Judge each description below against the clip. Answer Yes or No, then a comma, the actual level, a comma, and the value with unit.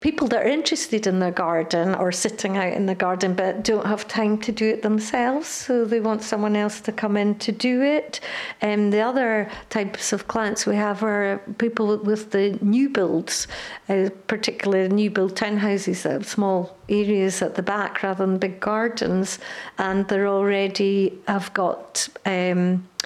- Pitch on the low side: No, high, 205 Hz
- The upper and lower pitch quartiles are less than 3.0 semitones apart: Yes, narrow, 2.4 semitones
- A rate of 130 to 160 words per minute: No, average, 180 wpm